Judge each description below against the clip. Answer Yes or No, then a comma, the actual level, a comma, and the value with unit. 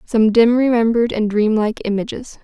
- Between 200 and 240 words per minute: No, average, 175 wpm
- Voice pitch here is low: No, high, 225 Hz